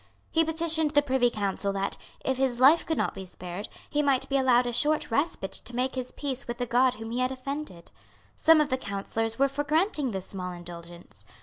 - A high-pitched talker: Yes, very high, 255 Hz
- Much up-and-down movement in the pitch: Yes, wide, 6.0 semitones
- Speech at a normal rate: No, fast, 215 wpm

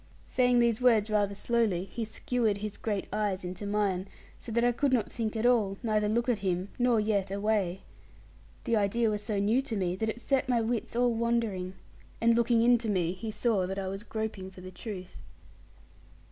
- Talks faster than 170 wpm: Yes, average, 200 wpm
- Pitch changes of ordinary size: Yes, average, 3.1 semitones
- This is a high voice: Yes, high, 215 Hz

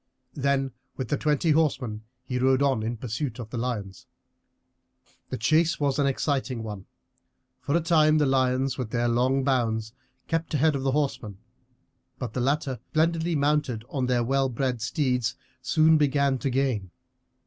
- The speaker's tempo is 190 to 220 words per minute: No, average, 160 wpm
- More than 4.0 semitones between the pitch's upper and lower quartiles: No, average, 3.3 semitones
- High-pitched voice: No, low, 135 Hz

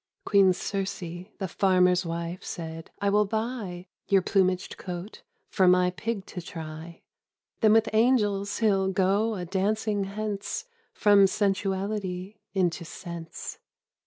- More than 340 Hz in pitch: No, high, 195 Hz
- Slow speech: Yes, slow, 130 wpm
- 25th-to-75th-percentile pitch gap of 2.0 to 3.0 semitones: Yes, narrow, 2.4 semitones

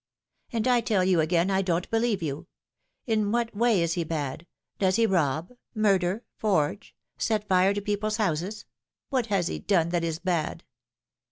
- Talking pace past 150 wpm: Yes, average, 175 wpm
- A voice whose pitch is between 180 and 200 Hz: Yes, high, 190 Hz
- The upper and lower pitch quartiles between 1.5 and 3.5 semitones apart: No, average, 4.2 semitones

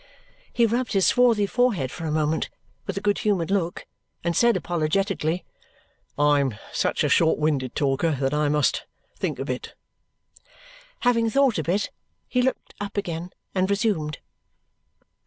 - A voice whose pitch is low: No, medium, 180 Hz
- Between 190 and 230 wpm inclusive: No, average, 155 wpm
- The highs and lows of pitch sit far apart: Yes, wide, 5.7 semitones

